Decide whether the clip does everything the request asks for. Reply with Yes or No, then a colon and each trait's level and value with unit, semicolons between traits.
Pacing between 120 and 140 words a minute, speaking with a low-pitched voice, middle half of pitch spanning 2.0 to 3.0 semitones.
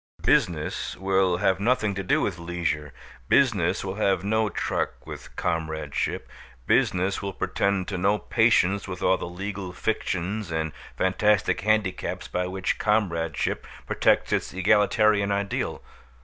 Yes: slow, 135 wpm; very low, 95 Hz; average, 2.7 semitones